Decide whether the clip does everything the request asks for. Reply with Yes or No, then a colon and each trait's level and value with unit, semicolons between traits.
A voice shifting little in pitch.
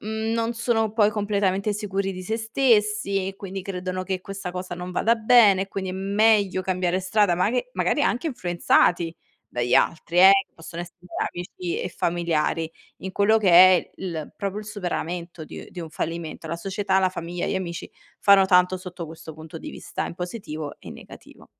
No: average, 3.1 semitones